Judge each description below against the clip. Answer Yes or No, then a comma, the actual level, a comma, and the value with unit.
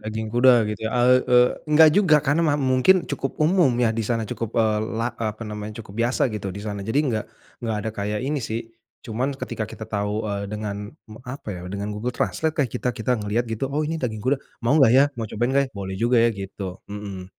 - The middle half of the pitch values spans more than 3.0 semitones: Yes, average, 3.8 semitones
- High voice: No, low, 115 Hz